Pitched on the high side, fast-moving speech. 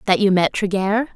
Yes: high, 200 Hz; fast, 210 wpm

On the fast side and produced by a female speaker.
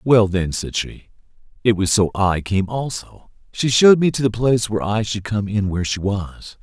No: fast, 215 wpm; male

